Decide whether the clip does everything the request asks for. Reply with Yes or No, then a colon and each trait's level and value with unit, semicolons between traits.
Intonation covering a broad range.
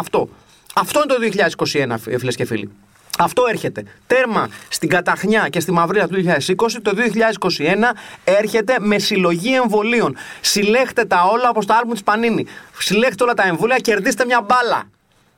Yes: wide, 5.7 semitones